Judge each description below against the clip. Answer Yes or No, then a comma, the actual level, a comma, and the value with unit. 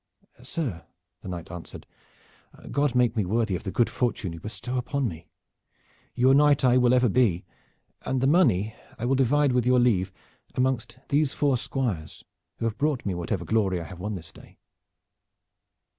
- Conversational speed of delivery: Yes, average, 175 wpm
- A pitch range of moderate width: No, wide, 5.9 semitones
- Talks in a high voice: No, low, 120 Hz